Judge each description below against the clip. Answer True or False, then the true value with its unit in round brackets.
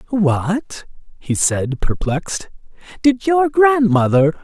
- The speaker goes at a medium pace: False (95 wpm)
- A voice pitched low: False (200 Hz)